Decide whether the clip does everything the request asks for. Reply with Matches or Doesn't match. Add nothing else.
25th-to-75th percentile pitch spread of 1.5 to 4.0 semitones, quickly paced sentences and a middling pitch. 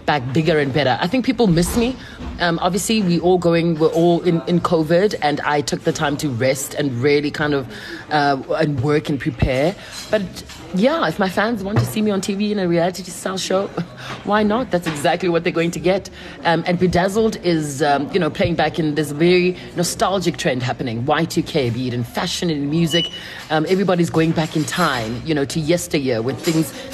Matches